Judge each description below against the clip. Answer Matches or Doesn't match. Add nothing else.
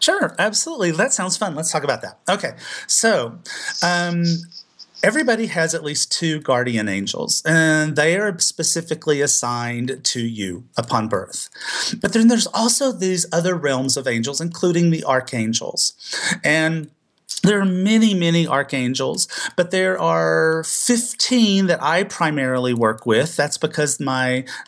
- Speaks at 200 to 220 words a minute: Doesn't match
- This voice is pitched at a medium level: Matches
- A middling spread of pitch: Doesn't match